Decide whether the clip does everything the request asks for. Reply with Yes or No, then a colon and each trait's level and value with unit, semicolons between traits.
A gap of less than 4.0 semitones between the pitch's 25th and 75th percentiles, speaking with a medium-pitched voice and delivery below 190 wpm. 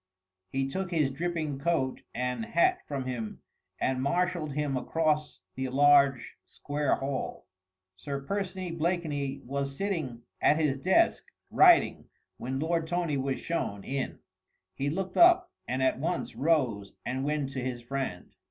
No: average, 4.3 semitones; medium, 145 Hz; average, 145 wpm